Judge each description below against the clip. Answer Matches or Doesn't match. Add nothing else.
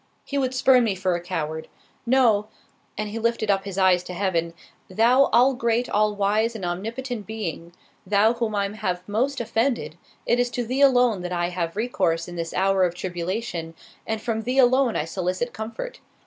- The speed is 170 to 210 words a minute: Matches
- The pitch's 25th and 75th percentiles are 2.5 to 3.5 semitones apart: Doesn't match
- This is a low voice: Doesn't match